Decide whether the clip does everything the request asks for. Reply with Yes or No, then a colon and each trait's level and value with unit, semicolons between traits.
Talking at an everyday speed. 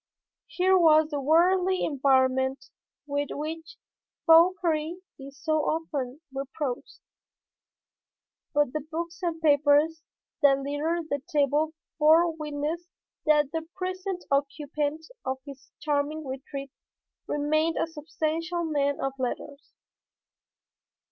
No: slow, 105 wpm